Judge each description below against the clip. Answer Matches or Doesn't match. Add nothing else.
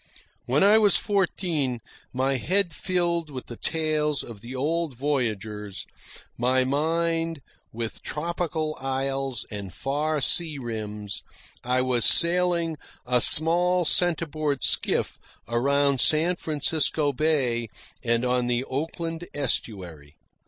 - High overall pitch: Doesn't match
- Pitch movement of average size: Matches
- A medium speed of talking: Doesn't match